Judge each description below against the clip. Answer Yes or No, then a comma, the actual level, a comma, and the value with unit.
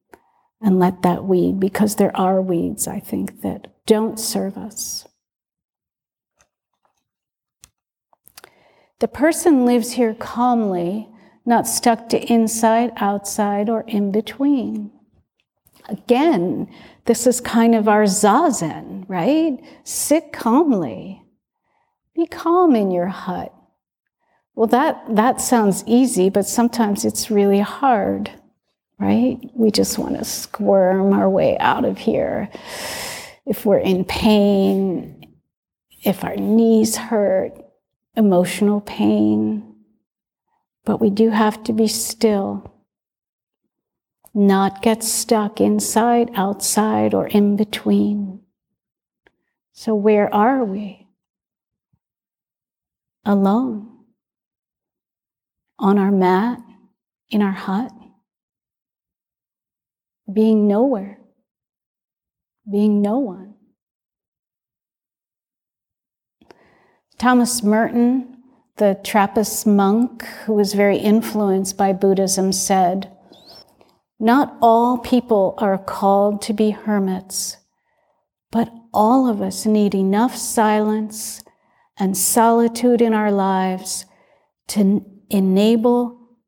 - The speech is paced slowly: Yes, slow, 95 wpm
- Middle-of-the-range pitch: No, high, 215 Hz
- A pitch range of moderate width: Yes, average, 3.1 semitones